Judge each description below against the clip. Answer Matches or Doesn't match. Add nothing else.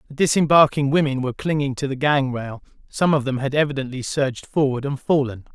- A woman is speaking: Doesn't match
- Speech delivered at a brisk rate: Doesn't match